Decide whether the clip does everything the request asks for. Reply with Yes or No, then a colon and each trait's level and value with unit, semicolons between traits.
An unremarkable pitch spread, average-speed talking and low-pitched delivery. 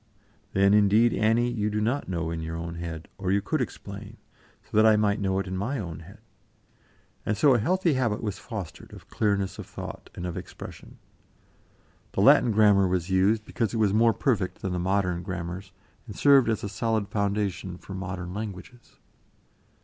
Yes: average, 3.1 semitones; average, 185 wpm; low, 100 Hz